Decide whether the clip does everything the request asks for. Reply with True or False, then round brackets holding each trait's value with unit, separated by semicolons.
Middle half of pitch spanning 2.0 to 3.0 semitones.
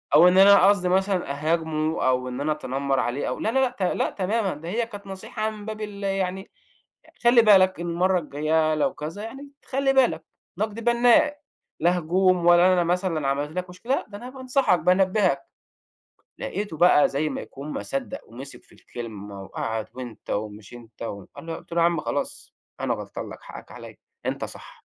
False (5.3 semitones)